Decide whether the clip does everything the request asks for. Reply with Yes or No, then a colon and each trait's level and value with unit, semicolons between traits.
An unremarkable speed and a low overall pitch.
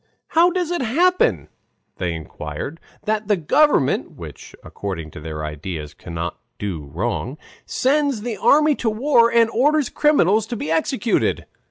No: average, 145 wpm; high, 210 Hz